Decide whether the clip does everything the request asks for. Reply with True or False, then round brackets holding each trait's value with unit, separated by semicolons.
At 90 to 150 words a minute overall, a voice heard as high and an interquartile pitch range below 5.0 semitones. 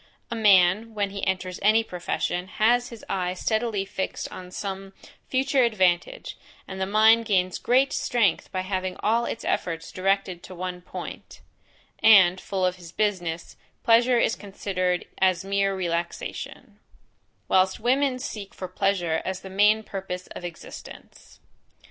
True (145 wpm; 195 Hz; 3.0 semitones)